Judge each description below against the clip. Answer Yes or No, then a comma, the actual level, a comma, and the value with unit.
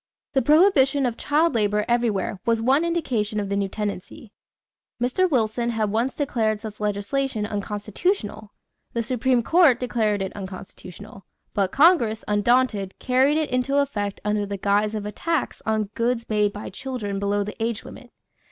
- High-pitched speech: Yes, high, 220 Hz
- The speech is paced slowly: No, average, 160 wpm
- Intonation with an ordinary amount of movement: Yes, average, 4.0 semitones